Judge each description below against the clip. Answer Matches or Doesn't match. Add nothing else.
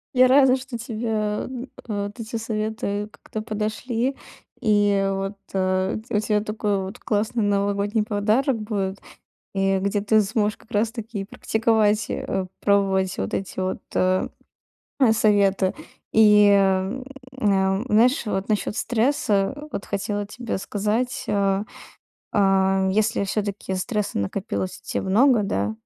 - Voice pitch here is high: Matches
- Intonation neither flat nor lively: Doesn't match